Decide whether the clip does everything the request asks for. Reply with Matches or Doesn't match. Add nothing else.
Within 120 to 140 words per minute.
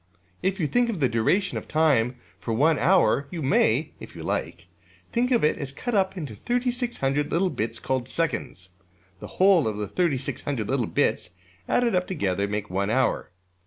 Doesn't match